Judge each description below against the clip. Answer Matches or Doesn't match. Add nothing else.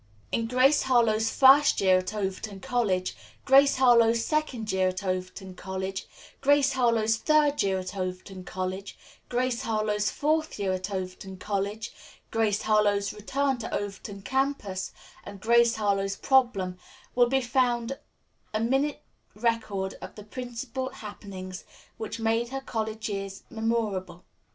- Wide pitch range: Doesn't match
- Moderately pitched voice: Doesn't match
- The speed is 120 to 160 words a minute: Matches